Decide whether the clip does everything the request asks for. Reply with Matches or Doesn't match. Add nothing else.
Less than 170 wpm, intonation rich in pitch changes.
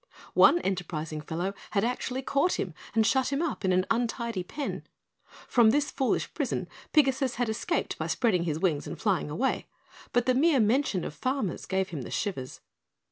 Doesn't match